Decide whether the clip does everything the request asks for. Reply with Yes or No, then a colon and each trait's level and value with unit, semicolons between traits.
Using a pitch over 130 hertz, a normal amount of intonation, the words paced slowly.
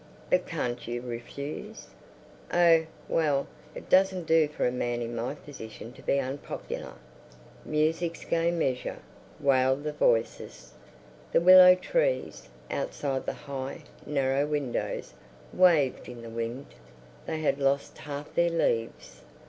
Yes: medium, 140 Hz; average, 4.8 semitones; slow, 130 wpm